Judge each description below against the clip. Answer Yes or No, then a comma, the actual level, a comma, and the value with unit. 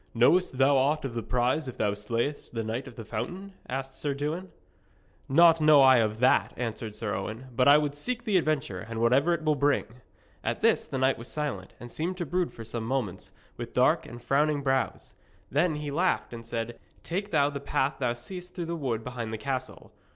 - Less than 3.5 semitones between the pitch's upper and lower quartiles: No, average, 4.5 semitones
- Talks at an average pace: No, fast, 210 wpm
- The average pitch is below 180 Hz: Yes, low, 135 Hz